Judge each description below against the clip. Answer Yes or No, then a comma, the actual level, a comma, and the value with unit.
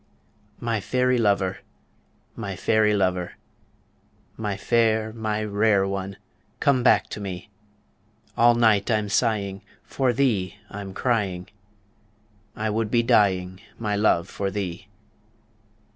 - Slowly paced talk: Yes, slow, 115 wpm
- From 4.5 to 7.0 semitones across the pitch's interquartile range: No, average, 2.7 semitones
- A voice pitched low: Yes, low, 105 Hz